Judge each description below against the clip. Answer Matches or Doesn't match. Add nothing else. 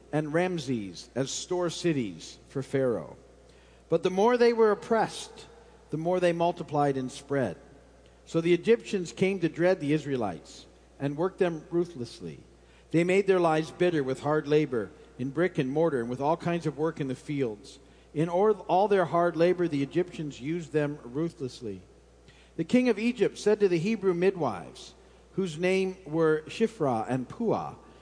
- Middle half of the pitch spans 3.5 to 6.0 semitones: Matches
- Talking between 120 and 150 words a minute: Doesn't match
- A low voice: Doesn't match